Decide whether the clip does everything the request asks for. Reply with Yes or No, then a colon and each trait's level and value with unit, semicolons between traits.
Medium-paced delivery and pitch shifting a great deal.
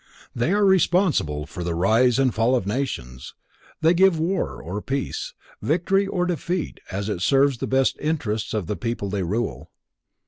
Yes: average, 170 wpm; wide, 8.5 semitones